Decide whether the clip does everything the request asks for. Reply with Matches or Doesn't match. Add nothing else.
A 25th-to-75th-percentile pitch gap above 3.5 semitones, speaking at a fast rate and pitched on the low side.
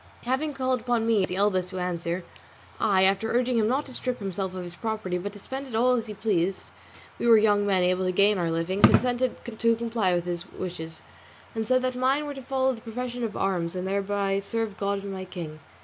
Doesn't match